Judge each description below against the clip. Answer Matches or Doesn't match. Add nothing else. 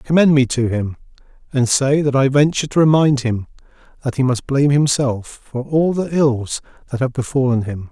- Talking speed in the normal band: Matches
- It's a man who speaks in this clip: Matches